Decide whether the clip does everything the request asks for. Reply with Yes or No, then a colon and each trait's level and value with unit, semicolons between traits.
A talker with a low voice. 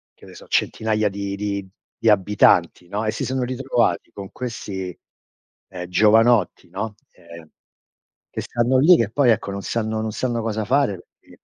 Yes: low, 110 Hz